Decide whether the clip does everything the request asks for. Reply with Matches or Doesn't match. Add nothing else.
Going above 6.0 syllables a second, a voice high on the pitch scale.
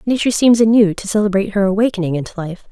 Matches